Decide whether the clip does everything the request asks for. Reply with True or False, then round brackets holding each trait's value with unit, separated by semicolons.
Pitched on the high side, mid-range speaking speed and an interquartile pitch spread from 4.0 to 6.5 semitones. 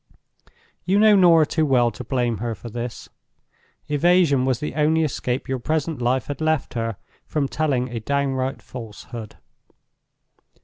False (135 Hz; 145 wpm; 4.5 semitones)